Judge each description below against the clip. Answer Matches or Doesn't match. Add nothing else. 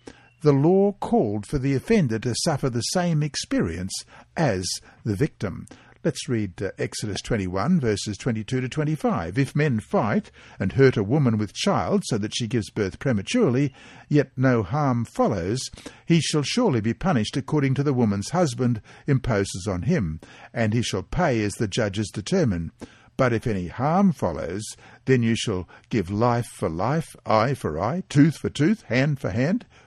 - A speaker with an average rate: Matches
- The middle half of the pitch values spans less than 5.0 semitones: Doesn't match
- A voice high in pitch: Doesn't match